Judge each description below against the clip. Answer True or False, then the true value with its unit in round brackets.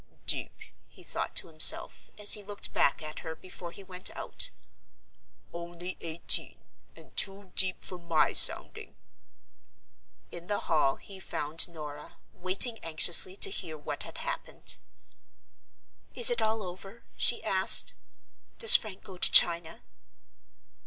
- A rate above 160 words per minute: False (135 wpm)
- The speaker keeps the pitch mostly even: False (3.3 semitones)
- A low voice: False (185 Hz)